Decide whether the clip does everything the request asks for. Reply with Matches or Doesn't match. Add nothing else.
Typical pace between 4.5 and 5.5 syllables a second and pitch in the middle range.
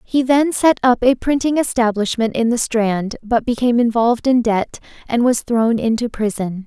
Doesn't match